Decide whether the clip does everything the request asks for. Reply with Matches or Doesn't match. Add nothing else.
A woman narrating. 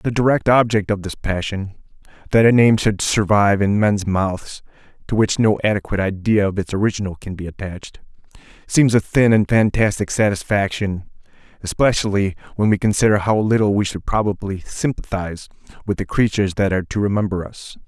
Doesn't match